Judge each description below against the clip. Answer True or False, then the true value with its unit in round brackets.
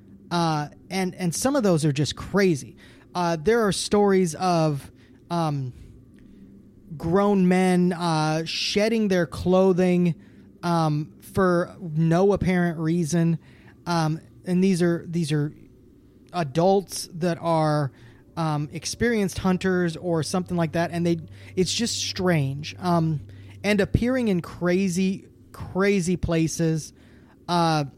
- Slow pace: True (120 wpm)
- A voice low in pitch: False (170 Hz)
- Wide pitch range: False (3.3 semitones)